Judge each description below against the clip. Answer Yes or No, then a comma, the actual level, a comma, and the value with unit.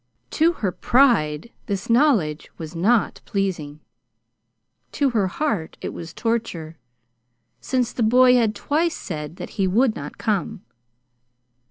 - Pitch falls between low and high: No, high, 215 Hz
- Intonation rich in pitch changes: Yes, wide, 6.8 semitones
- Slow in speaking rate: Yes, slow, 130 wpm